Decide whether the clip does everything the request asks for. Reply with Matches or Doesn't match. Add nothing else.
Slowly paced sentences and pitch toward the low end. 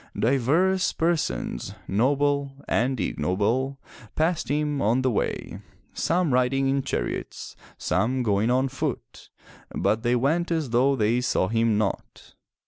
Matches